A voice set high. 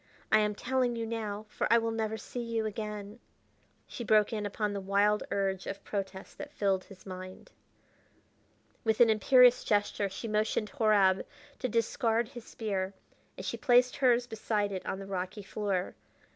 Yes: high, 215 Hz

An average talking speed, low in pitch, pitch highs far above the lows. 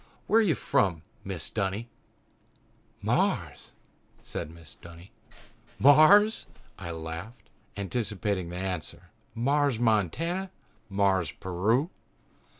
No: slow, 95 wpm; low, 100 Hz; wide, 7.6 semitones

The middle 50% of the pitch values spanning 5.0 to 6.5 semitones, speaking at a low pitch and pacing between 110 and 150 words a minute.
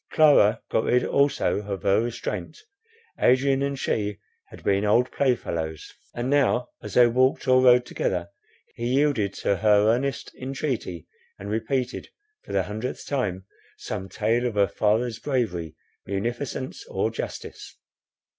No: average, 4.1 semitones; low, 120 Hz; average, 140 wpm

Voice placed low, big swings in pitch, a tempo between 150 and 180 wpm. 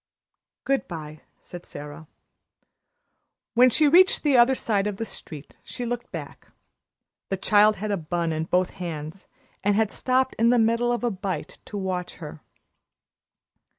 No: high, 205 Hz; wide, 5.7 semitones; average, 155 wpm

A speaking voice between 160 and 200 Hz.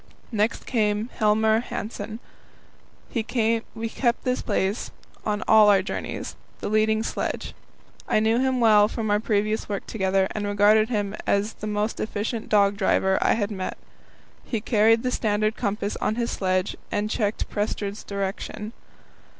No: high, 215 Hz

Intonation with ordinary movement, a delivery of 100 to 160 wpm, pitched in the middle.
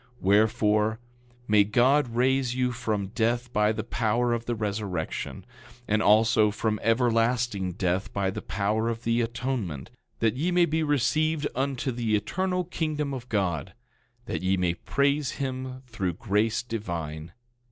No: average, 3.8 semitones; average, 150 wpm; low, 115 Hz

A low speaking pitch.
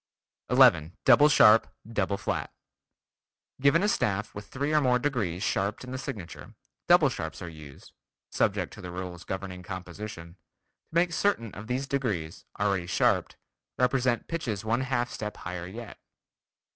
Yes: low, 105 Hz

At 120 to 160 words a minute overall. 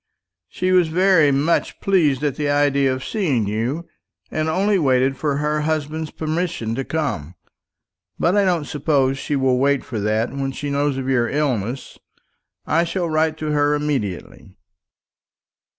Yes: average, 155 wpm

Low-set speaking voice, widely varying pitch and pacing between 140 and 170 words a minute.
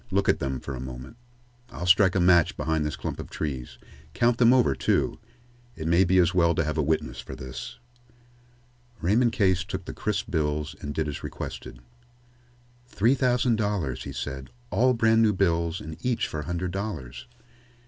No: very low, 85 Hz; wide, 5.9 semitones; average, 185 wpm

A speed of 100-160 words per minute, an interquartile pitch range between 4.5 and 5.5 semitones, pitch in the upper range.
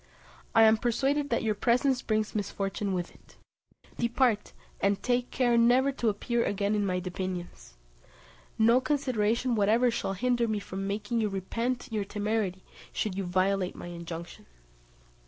No: average, 150 wpm; average, 3.6 semitones; high, 215 Hz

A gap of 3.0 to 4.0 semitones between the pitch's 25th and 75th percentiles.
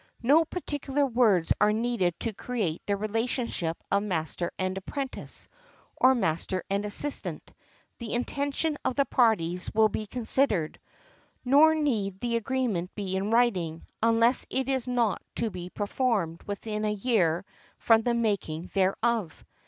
No: average, 4.7 semitones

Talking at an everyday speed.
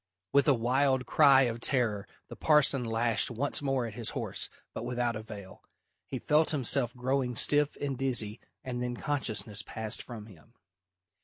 Yes: average, 160 wpm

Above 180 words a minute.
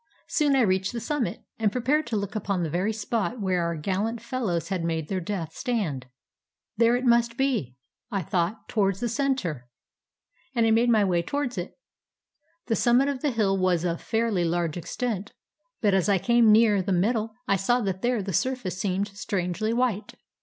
Yes: average, 190 wpm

